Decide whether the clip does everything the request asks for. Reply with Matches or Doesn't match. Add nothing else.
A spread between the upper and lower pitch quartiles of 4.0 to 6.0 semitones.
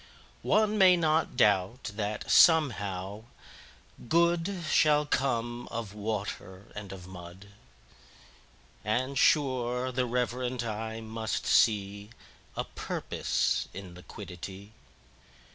Matches